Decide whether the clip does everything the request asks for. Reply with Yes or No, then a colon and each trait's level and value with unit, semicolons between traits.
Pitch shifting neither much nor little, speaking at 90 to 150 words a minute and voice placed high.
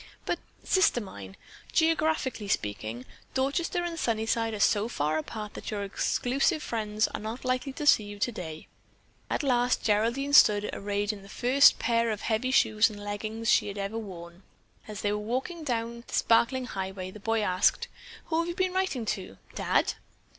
No: average, 4.1 semitones; average, 175 wpm; high, 225 Hz